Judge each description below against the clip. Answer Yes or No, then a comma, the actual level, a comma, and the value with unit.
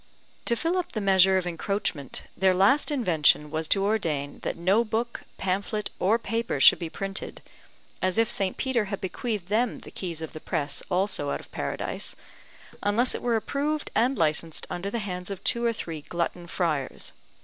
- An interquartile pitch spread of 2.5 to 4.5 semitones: No, average, 5.0 semitones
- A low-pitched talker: No, high, 195 Hz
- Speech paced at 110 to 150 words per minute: No, average, 180 wpm